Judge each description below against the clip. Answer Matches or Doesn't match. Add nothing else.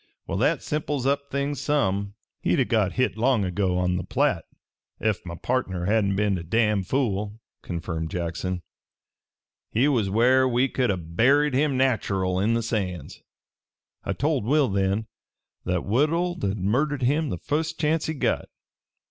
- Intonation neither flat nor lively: Doesn't match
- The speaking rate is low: Doesn't match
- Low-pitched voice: Matches